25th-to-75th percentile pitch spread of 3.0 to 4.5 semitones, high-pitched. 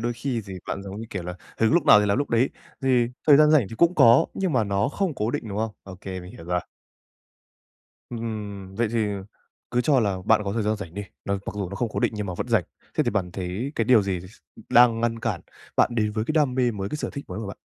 No: average, 3.8 semitones; low, 110 Hz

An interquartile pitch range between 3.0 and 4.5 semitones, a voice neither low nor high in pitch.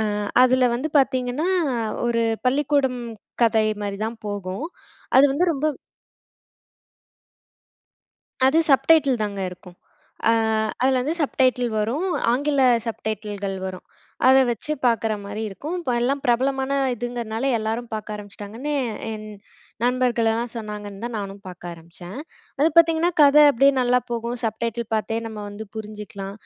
No: average, 3.9 semitones; high, 235 Hz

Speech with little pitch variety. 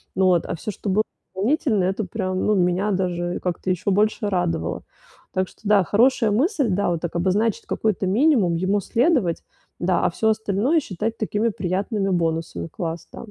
No: average, 3.5 semitones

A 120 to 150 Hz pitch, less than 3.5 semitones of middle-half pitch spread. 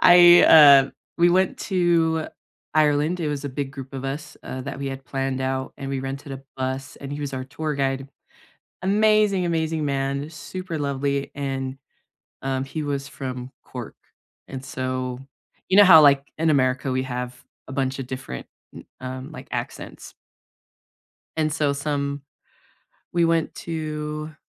Yes: medium, 140 Hz; average, 2.9 semitones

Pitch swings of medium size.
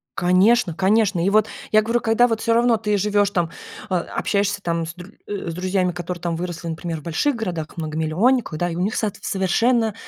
Yes: average, 4.1 semitones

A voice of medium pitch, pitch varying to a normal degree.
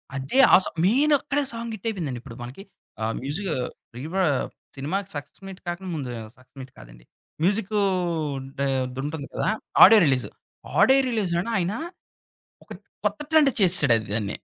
No: medium, 175 Hz; wide, 8.0 semitones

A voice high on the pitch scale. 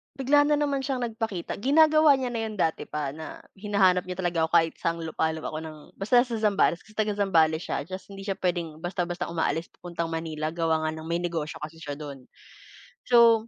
No: medium, 175 Hz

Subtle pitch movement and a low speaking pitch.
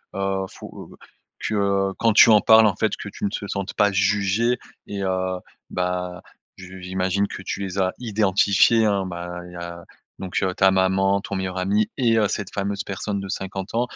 Yes: narrow, 1.7 semitones; very low, 95 Hz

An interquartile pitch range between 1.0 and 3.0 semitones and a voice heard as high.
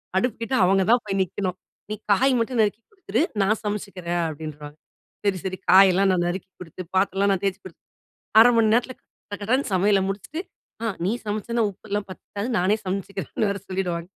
Yes: narrow, 2.4 semitones; high, 195 Hz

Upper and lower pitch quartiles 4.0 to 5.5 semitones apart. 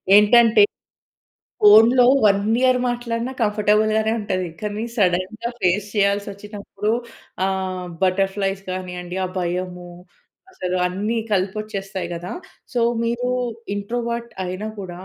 No: average, 3.0 semitones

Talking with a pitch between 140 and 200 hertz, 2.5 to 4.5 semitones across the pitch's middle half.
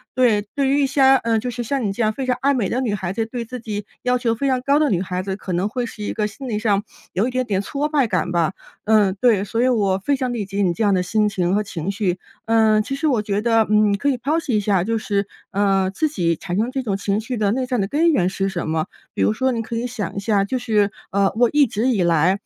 No: high, 215 Hz; average, 4.1 semitones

